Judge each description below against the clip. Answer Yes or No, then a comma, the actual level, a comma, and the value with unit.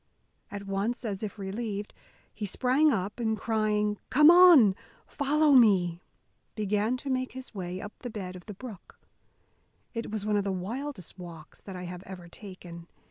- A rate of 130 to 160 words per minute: No, average, 170 wpm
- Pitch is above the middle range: Yes, high, 210 Hz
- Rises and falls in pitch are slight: No, average, 4.5 semitones